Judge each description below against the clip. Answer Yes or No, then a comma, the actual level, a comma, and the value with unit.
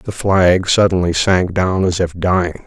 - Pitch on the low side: Yes, very low, 90 Hz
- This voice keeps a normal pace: Yes, average, 180 wpm